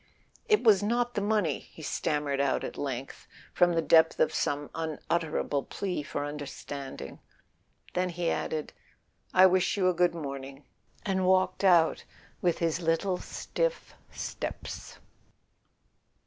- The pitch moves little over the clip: No, average, 4.2 semitones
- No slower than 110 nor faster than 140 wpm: Yes, slow, 135 wpm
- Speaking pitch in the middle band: Yes, medium, 165 Hz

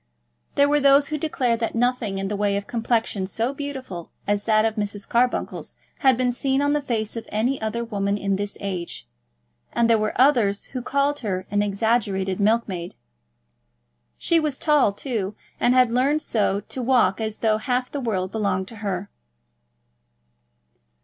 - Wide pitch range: No, average, 4.1 semitones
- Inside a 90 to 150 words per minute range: No, average, 170 wpm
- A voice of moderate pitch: No, high, 225 Hz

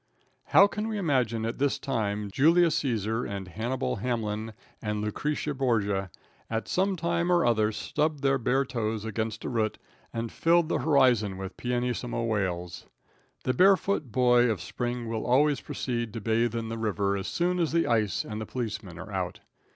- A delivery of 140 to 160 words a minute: No, average, 175 wpm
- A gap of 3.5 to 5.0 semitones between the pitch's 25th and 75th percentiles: Yes, average, 4.5 semitones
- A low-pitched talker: Yes, low, 115 Hz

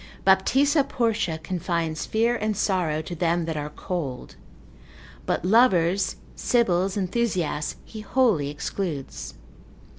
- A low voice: No, medium, 185 Hz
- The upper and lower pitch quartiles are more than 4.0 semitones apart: Yes, average, 5.2 semitones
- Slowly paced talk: Yes, slow, 110 wpm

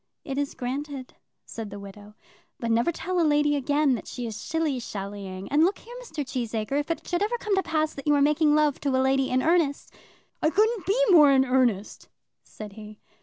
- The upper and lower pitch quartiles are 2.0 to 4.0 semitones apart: No, average, 5.1 semitones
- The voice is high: Yes, very high, 280 Hz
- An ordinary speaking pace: No, fast, 220 wpm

